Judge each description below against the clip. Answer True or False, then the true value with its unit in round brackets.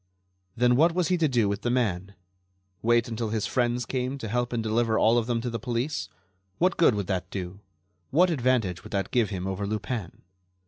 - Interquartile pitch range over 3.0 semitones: True (3.5 semitones)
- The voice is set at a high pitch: False (115 Hz)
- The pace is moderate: False (215 wpm)